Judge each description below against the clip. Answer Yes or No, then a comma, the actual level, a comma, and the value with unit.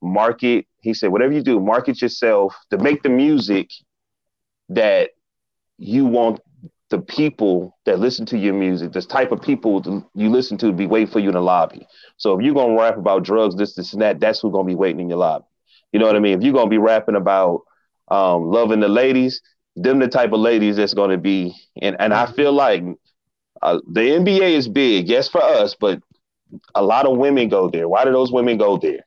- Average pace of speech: No, fast, 215 wpm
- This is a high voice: No, low, 110 Hz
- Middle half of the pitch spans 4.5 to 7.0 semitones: Yes, average, 4.9 semitones